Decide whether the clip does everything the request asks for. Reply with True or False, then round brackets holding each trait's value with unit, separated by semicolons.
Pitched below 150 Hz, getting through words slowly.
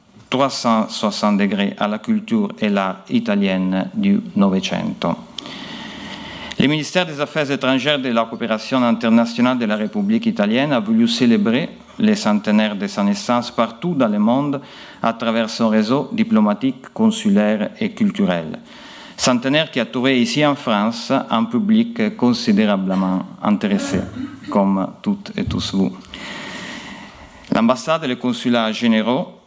True (140 Hz; 130 wpm)